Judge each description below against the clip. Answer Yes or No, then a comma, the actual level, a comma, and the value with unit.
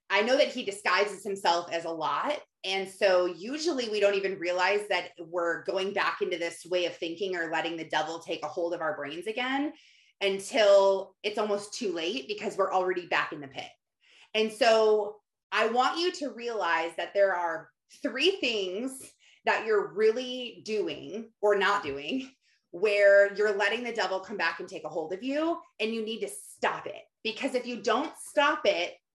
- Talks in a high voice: Yes, high, 205 Hz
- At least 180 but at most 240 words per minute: Yes, average, 190 wpm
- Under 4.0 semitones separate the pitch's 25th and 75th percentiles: No, average, 4.6 semitones